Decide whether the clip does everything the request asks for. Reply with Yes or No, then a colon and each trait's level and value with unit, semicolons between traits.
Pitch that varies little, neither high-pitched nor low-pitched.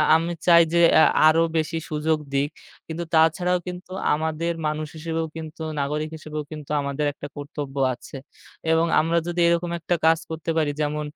Yes: narrow, 1.7 semitones; medium, 160 Hz